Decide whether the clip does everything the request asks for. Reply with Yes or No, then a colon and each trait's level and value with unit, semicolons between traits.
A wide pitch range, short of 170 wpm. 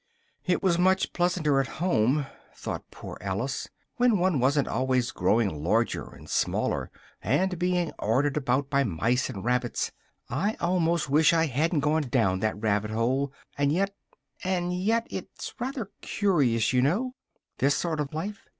Yes: wide, 6.4 semitones; average, 155 wpm